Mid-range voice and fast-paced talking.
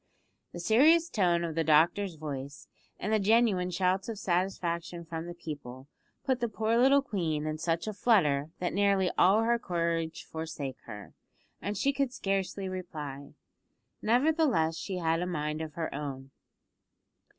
No: medium, 175 Hz; average, 155 wpm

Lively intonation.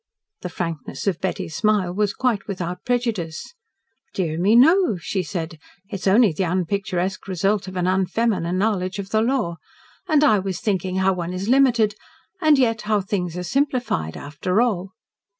No: average, 3.7 semitones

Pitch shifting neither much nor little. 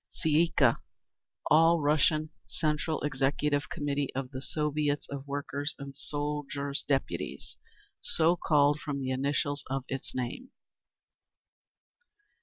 No: narrow, 1.6 semitones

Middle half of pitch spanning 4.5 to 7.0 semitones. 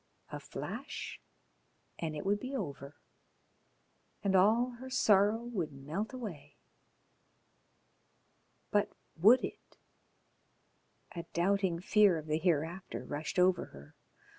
Yes: average, 5.2 semitones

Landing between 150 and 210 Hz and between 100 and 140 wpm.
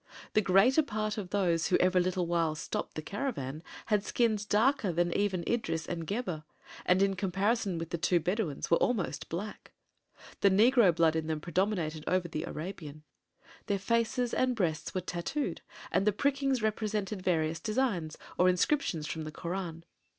No: medium, 185 Hz; average, 165 wpm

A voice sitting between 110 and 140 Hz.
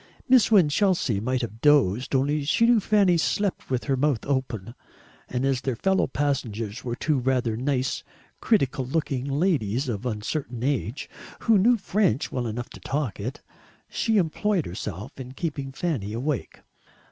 Yes: low, 135 Hz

